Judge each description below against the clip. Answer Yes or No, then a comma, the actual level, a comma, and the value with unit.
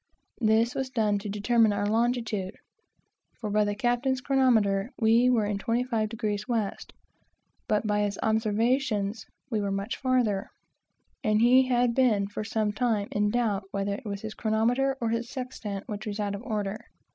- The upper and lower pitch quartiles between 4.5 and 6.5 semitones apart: No, average, 2.8 semitones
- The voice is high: Yes, high, 220 Hz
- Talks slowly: No, average, 165 wpm